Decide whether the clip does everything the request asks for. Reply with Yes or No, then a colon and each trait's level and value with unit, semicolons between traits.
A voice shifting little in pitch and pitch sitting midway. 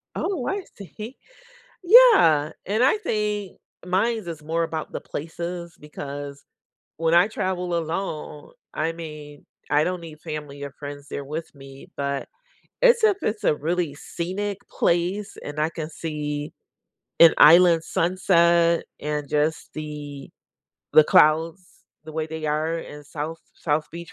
No: average, 3.3 semitones; medium, 165 Hz